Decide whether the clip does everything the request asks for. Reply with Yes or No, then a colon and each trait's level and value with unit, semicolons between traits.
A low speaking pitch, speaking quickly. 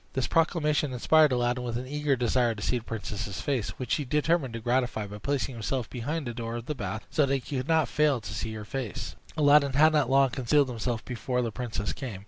Yes: low, 125 Hz; fast, 230 wpm